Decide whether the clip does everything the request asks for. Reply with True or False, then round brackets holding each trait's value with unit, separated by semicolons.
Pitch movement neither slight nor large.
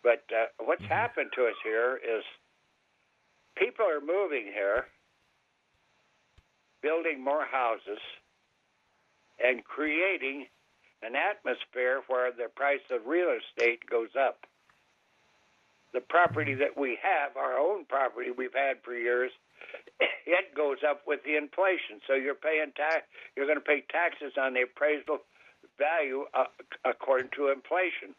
False (5.9 semitones)